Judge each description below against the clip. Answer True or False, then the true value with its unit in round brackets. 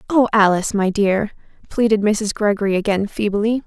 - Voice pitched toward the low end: False (210 Hz)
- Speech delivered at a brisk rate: False (145 wpm)